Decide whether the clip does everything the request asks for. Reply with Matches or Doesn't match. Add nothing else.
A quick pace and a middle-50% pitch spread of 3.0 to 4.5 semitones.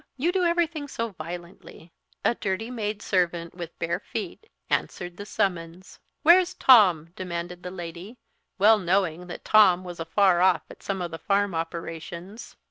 Doesn't match